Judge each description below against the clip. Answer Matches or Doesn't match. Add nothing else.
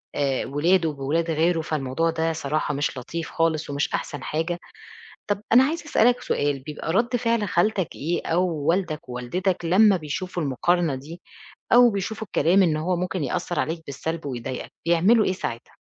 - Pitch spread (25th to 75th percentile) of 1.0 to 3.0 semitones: Doesn't match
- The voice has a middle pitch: Matches